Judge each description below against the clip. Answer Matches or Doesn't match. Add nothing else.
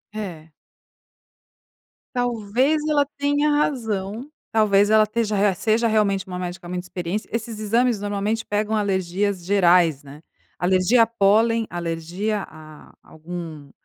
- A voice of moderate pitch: Doesn't match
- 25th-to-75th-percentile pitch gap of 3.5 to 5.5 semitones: Matches